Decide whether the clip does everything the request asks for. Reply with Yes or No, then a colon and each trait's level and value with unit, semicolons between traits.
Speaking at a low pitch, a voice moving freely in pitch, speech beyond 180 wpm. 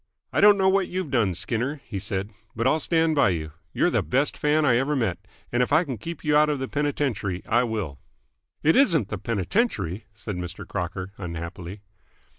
Yes: low, 120 Hz; wide, 7.8 semitones; average, 200 wpm